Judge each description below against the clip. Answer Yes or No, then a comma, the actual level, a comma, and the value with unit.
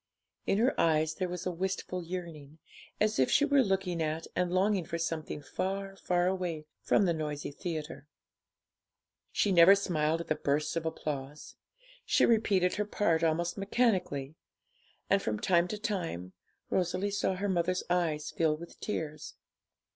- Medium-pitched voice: Yes, medium, 175 Hz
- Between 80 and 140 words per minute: No, average, 155 wpm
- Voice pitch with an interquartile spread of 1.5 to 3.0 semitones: No, average, 3.6 semitones